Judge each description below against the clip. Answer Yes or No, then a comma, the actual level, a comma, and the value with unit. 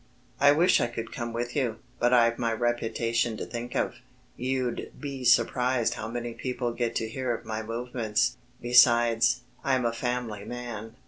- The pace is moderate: Yes, average, 165 wpm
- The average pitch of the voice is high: No, low, 120 Hz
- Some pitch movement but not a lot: No, narrow, 1.4 semitones